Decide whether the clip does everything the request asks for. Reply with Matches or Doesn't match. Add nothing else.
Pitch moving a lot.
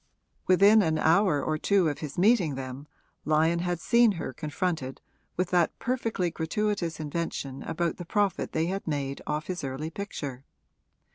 Doesn't match